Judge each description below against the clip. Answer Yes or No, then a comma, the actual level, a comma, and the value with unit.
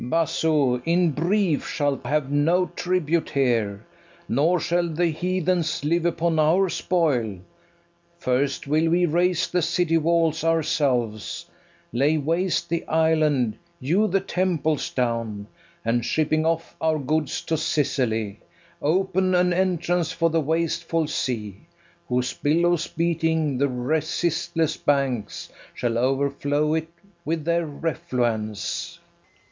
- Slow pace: Yes, slow, 120 wpm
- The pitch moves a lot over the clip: No, average, 3.8 semitones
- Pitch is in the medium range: Yes, medium, 155 Hz